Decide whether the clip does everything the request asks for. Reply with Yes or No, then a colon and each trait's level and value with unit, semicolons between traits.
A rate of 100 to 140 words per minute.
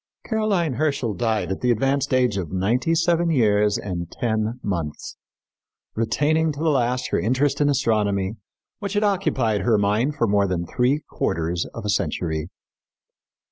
No: average, 155 wpm